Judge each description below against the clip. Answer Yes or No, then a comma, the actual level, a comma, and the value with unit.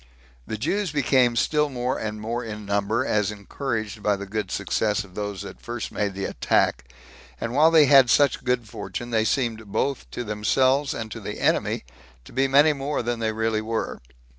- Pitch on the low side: Yes, low, 115 Hz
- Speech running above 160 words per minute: Yes, average, 190 wpm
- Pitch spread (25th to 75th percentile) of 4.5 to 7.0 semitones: No, average, 4.0 semitones